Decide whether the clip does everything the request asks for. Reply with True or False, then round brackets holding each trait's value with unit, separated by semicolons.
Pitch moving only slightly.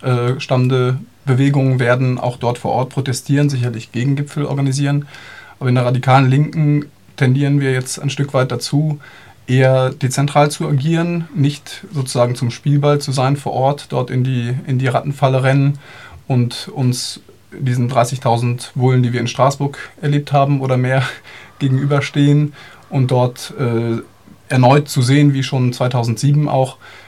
True (2.2 semitones)